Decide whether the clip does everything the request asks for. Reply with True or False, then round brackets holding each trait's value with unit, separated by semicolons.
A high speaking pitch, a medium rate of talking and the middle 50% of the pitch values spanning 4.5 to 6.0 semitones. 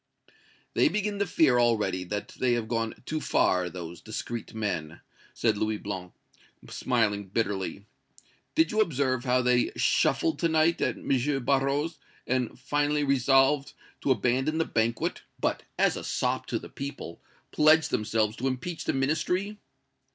False (125 Hz; 150 wpm; 5.5 semitones)